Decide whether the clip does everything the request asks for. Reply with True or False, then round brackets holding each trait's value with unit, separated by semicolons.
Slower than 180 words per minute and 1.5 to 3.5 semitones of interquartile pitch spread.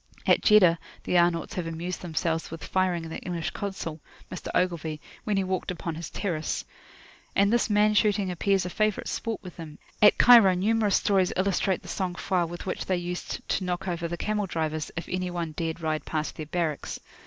False (200 wpm; 2.9 semitones)